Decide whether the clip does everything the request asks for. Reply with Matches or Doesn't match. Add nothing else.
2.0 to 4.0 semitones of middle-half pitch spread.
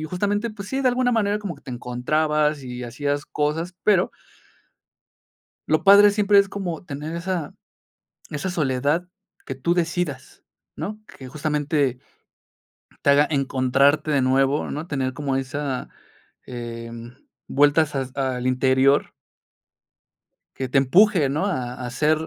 Doesn't match